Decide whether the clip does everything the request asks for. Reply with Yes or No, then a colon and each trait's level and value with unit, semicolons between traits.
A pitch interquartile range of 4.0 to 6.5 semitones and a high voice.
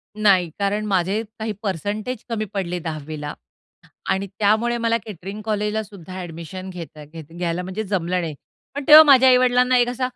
Yes: average, 4.3 semitones; high, 200 Hz